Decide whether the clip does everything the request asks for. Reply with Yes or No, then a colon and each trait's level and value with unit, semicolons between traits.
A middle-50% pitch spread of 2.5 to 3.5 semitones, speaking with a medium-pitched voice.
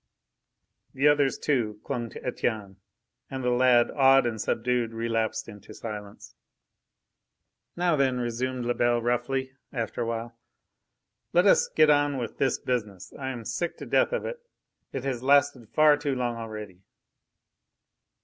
No: average, 3.0 semitones; low, 125 Hz